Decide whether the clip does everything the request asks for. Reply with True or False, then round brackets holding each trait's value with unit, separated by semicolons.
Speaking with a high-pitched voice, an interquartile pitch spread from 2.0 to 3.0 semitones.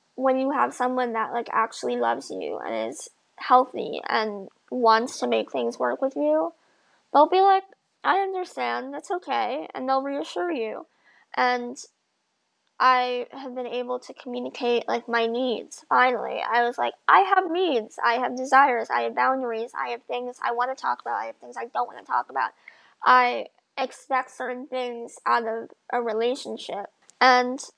True (250 Hz; 2.4 semitones)